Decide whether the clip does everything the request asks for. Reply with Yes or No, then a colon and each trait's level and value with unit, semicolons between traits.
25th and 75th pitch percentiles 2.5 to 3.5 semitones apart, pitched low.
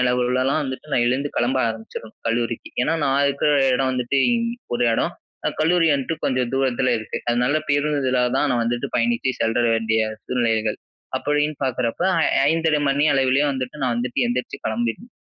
Yes: average, 2.8 semitones; low, 130 Hz